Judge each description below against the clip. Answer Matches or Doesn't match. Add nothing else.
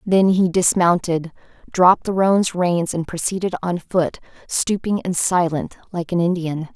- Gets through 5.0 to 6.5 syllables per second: Doesn't match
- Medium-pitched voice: Matches